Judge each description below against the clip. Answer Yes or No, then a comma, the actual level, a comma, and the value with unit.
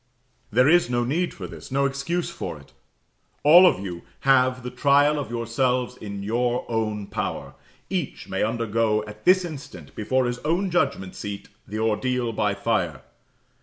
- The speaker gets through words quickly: No, average, 165 wpm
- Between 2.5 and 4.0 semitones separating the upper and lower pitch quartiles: No, average, 4.7 semitones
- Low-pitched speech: Yes, low, 120 Hz